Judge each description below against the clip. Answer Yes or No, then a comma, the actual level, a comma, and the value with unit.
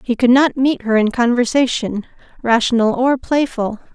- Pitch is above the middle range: Yes, high, 245 Hz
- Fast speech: No, average, 150 wpm